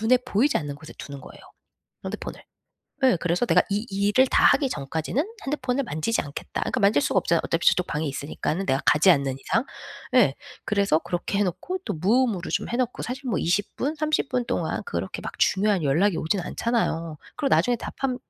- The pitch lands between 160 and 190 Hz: No, high, 200 Hz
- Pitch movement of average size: No, wide, 7.6 semitones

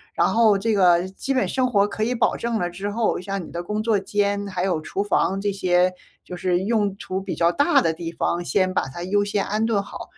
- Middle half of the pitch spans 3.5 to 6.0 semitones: No, average, 2.9 semitones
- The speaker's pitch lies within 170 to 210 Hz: Yes, high, 200 Hz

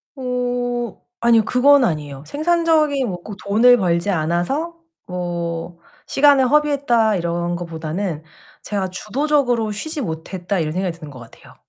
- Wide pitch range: Yes, wide, 7.4 semitones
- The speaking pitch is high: Yes, high, 210 Hz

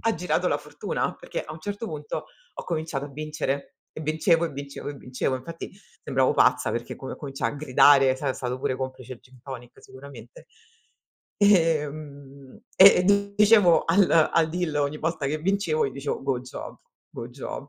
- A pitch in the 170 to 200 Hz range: No, medium, 145 Hz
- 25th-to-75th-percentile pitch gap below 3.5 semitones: No, average, 3.8 semitones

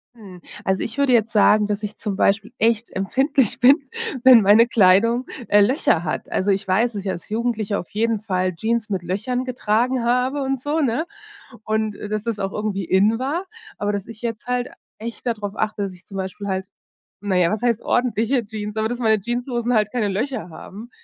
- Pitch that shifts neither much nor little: Yes, average, 3.2 semitones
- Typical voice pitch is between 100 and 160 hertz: No, high, 220 Hz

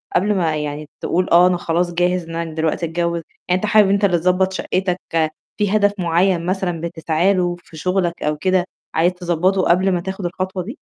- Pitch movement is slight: Yes, narrow, 1.9 semitones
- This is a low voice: No, medium, 180 Hz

